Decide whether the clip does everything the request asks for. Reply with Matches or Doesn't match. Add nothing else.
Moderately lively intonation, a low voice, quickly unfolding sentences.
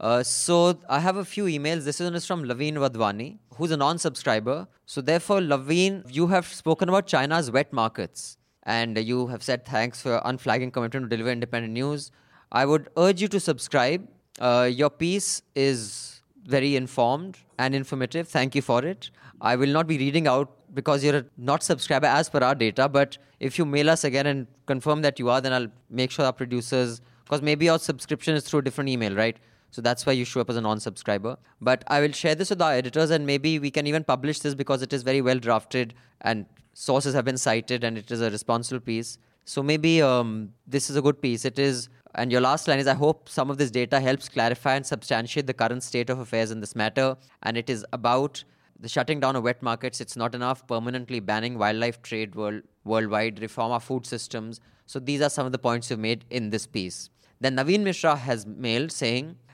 Matches